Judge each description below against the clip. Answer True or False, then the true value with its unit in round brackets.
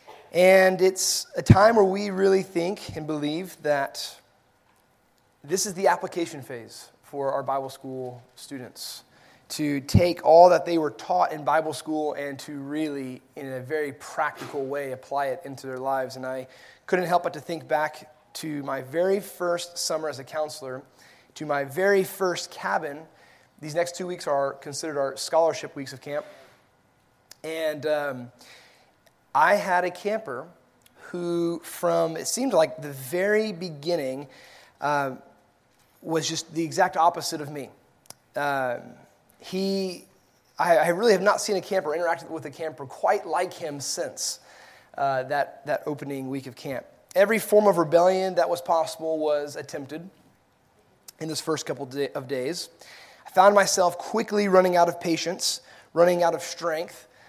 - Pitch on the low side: False (155 Hz)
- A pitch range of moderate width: True (4.1 semitones)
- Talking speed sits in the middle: True (160 wpm)